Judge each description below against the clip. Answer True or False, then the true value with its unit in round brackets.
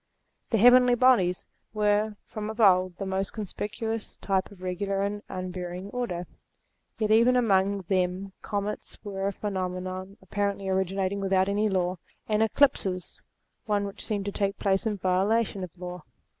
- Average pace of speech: True (150 wpm)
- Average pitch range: False (2.2 semitones)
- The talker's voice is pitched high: True (195 Hz)